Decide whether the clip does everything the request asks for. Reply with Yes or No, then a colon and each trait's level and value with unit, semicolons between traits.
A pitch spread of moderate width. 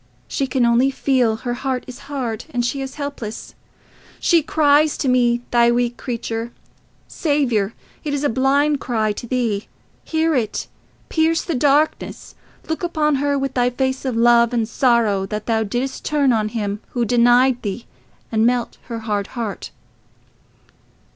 Yes: average, 3.3 semitones